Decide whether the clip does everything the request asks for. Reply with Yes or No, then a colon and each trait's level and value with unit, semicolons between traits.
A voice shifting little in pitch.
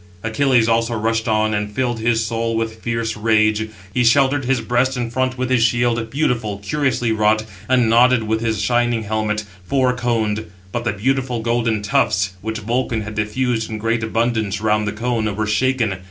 Yes: narrow, 2.1 semitones